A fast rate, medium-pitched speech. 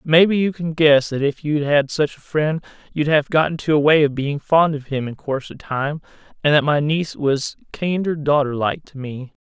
Yes: fast, 230 wpm; medium, 150 Hz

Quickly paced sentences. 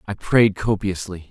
No: average, 140 wpm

